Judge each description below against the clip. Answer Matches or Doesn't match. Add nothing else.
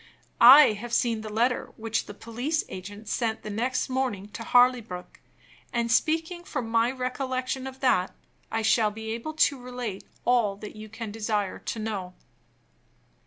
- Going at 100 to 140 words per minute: Doesn't match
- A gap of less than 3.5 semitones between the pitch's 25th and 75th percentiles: Matches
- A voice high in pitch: Matches